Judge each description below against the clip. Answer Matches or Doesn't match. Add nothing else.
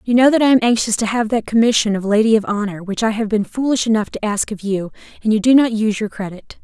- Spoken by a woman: Matches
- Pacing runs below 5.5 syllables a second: Doesn't match